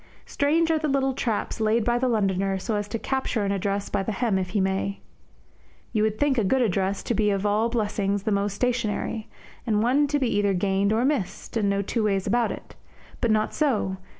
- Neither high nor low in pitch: No, high, 215 Hz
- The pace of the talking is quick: Yes, fast, 220 wpm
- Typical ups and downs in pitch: Yes, average, 3.5 semitones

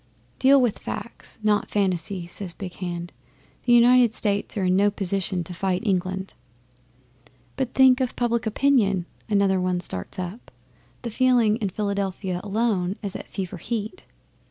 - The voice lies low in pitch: No, high, 200 Hz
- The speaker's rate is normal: Yes, average, 150 wpm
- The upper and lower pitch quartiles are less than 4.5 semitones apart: Yes, average, 4.1 semitones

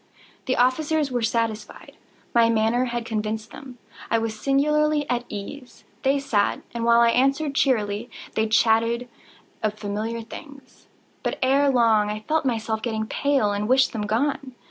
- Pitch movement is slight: No, average, 3.7 semitones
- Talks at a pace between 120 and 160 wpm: Yes, average, 155 wpm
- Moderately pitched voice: No, high, 235 Hz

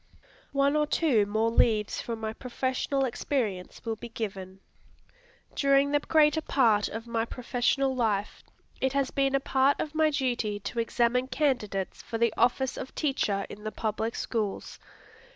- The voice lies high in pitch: Yes, high, 240 Hz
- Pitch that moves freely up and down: No, average, 4.0 semitones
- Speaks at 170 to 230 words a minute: No, average, 155 wpm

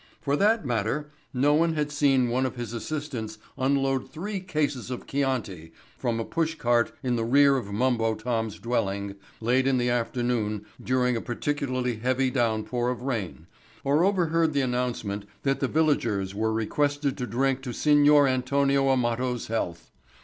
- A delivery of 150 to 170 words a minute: Yes, average, 165 wpm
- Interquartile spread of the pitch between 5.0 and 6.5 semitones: No, average, 3.6 semitones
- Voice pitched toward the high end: No, low, 125 Hz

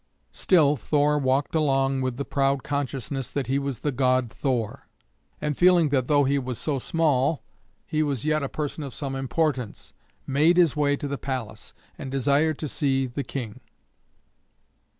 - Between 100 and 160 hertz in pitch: Yes, medium, 140 Hz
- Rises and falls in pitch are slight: Yes, narrow, 2.1 semitones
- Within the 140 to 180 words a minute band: Yes, average, 170 wpm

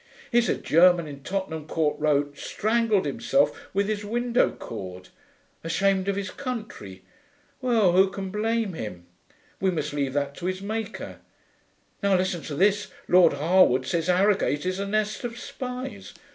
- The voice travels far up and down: Yes, wide, 5.7 semitones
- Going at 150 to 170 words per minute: Yes, average, 155 wpm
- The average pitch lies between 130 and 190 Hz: Yes, medium, 185 Hz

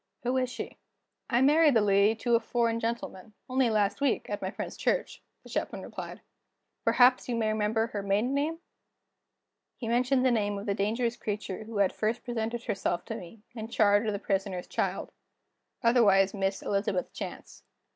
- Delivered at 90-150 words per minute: No, average, 175 wpm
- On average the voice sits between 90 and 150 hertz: No, high, 220 Hz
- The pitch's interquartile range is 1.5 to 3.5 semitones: Yes, average, 3.1 semitones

